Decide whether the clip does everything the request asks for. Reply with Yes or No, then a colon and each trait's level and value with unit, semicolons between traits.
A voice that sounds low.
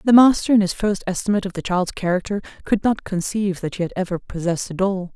No: high, 190 Hz